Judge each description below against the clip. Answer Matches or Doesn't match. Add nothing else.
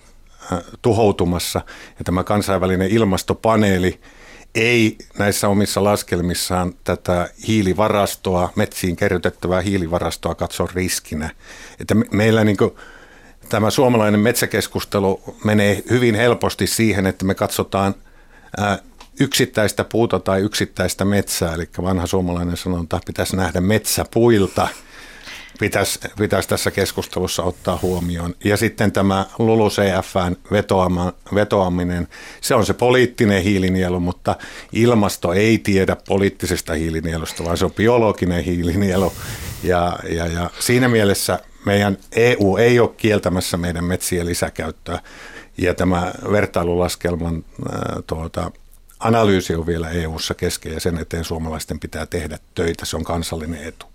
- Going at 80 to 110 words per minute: Doesn't match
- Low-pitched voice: Matches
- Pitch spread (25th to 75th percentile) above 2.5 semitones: Matches